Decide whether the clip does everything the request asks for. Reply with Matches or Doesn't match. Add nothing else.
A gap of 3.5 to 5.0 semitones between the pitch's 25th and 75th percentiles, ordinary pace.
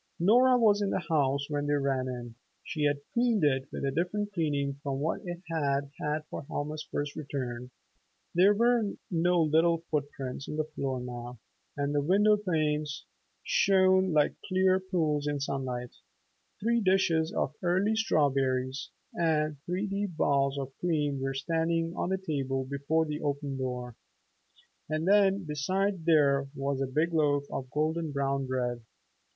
Matches